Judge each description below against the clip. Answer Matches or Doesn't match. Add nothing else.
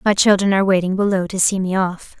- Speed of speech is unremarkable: Doesn't match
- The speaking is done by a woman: Matches